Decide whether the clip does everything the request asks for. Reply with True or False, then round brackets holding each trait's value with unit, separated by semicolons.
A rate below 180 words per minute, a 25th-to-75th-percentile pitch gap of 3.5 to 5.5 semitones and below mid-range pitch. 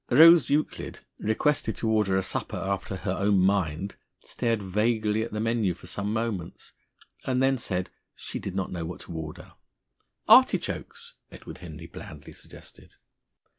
True (155 wpm; 3.8 semitones; 100 Hz)